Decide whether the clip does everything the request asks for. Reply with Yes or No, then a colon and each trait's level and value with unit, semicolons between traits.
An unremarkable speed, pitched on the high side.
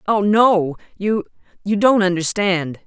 No: slow, 85 wpm; high, 195 Hz